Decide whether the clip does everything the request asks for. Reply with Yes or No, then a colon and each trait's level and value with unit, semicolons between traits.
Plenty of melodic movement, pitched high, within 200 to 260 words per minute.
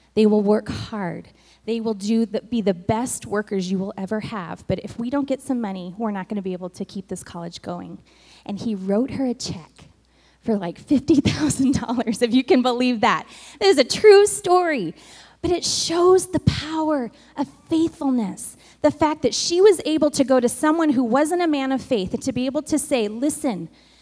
Yes: wide, 6.1 semitones; very high, 250 Hz; fast, 205 wpm